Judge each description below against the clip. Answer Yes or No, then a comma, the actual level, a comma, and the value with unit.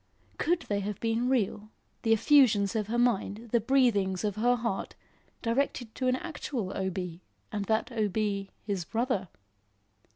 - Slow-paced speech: No, average, 160 wpm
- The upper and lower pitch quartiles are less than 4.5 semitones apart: Yes, average, 3.5 semitones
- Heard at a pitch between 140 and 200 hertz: No, high, 220 Hz